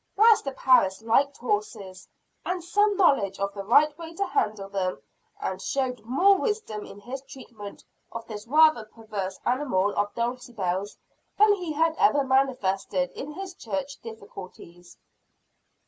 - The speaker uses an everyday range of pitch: No, wide, 7.6 semitones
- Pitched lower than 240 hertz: No, very high, 255 Hz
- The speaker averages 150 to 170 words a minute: No, average, 140 wpm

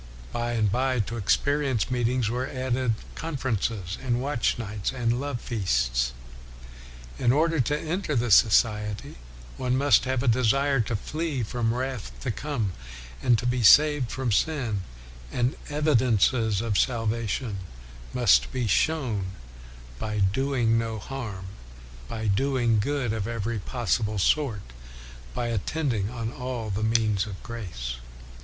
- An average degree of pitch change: Yes, average, 3.6 semitones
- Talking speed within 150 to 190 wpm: No, average, 140 wpm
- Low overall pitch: Yes, low, 120 Hz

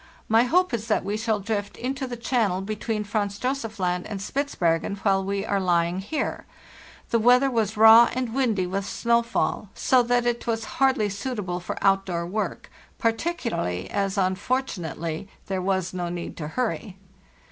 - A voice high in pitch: Yes, high, 210 Hz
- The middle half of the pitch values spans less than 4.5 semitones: Yes, average, 3.9 semitones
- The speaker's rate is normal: Yes, average, 160 wpm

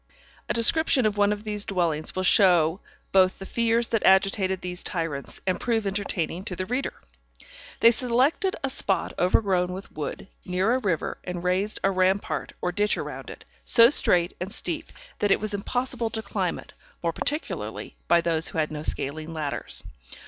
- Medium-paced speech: Yes, average, 180 wpm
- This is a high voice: Yes, high, 195 Hz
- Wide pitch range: No, average, 3.9 semitones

